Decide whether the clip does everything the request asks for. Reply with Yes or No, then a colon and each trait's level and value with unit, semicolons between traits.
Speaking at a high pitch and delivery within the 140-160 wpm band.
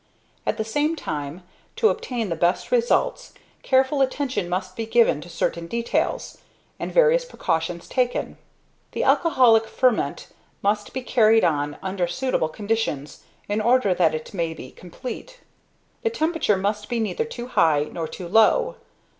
Yes: high, 220 Hz; average, 150 wpm